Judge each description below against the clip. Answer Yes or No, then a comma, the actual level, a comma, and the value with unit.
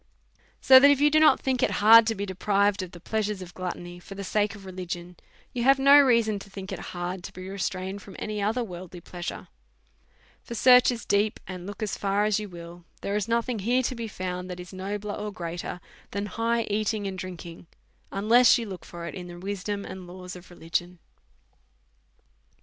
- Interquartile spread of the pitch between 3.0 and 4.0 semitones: Yes, average, 3.3 semitones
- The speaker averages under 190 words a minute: No, fast, 205 wpm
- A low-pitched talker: No, high, 200 Hz